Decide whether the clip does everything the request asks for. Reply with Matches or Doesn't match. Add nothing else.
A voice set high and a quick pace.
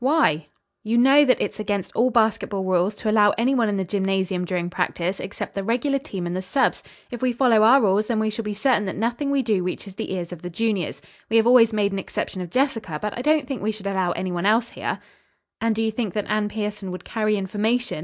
Matches